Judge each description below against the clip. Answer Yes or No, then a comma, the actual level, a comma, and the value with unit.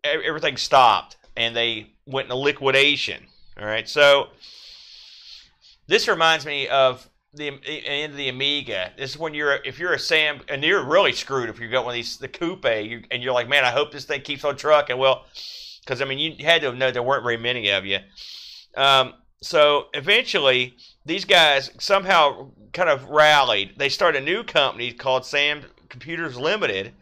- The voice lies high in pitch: No, low, 135 Hz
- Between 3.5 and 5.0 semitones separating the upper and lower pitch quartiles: No, average, 3.0 semitones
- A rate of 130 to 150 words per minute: No, average, 180 wpm